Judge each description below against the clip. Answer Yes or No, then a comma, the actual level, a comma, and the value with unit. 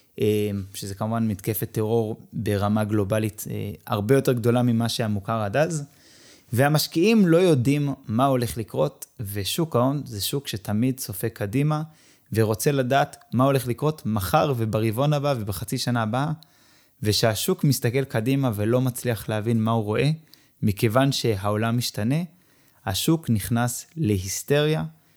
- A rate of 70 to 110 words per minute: No, average, 125 wpm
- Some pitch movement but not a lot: Yes, average, 4.5 semitones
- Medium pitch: No, low, 120 Hz